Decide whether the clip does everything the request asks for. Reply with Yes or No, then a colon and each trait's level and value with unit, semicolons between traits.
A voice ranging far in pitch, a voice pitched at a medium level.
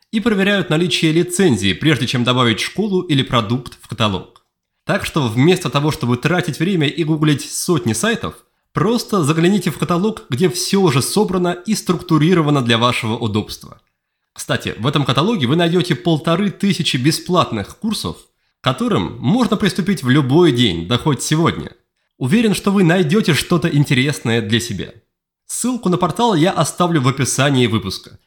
Yes: wide, 6.6 semitones; medium, 160 Hz